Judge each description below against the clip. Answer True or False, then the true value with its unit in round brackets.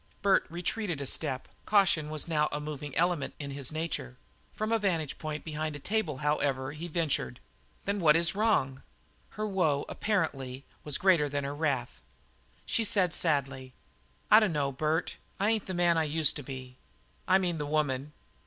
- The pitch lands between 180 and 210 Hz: False (155 Hz)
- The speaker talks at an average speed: True (170 wpm)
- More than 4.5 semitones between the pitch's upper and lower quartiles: False (4.0 semitones)